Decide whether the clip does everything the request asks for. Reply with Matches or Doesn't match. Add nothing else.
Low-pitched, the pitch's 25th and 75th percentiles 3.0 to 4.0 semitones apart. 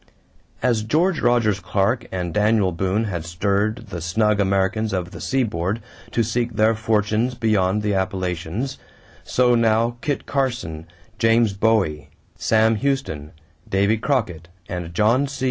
Matches